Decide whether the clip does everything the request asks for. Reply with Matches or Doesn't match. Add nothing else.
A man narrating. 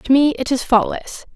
Doesn't match